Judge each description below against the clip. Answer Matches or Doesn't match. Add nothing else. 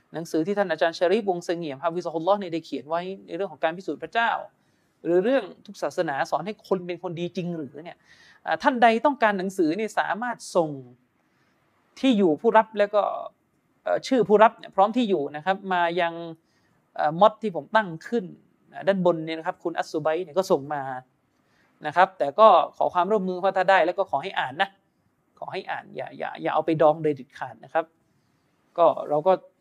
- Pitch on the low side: Doesn't match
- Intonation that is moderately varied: Matches